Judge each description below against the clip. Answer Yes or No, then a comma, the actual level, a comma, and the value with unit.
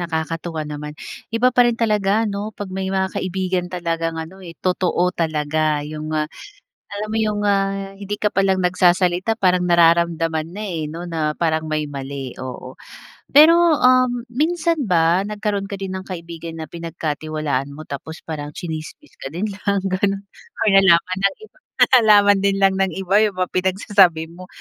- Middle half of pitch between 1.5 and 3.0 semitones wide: No, average, 3.8 semitones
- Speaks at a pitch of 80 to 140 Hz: No, medium, 185 Hz